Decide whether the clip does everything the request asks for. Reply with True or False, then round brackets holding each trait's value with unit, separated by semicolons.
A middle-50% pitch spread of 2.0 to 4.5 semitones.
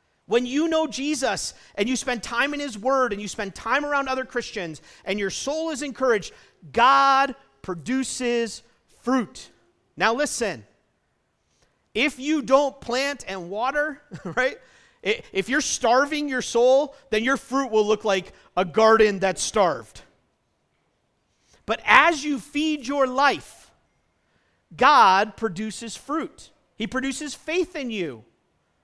False (5.0 semitones)